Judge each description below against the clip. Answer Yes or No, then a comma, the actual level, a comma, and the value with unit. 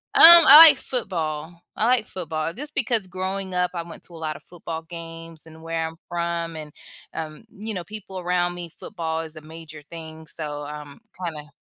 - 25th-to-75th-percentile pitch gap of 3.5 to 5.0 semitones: No, average, 2.8 semitones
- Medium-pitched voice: Yes, medium, 165 Hz